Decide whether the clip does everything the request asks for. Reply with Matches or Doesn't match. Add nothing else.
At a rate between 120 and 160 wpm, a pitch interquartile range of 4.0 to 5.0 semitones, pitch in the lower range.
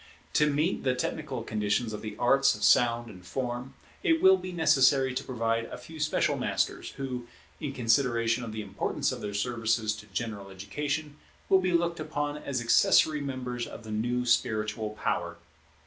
Doesn't match